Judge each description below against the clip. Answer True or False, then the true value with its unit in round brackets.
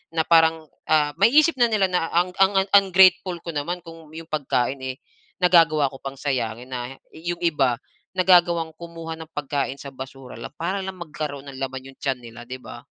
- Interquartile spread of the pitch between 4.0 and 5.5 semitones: True (4.7 semitones)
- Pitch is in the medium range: True (160 Hz)